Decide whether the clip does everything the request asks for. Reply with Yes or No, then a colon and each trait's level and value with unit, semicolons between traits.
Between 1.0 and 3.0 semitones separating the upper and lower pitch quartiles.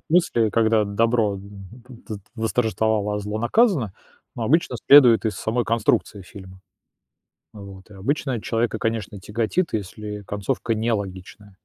Yes: narrow, 2.5 semitones